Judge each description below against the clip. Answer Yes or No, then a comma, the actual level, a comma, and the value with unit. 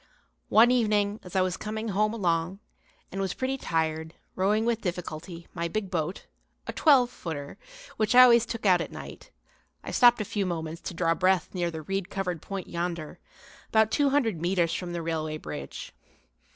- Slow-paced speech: No, average, 180 wpm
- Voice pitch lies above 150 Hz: Yes, medium, 185 Hz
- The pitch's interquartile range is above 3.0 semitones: Yes, average, 4.5 semitones